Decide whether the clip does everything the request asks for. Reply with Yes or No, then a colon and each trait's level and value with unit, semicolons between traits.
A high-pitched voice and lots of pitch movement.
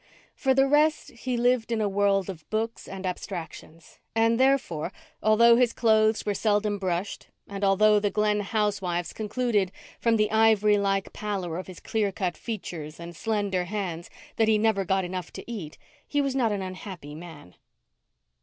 No: high, 205 Hz; average, 3.2 semitones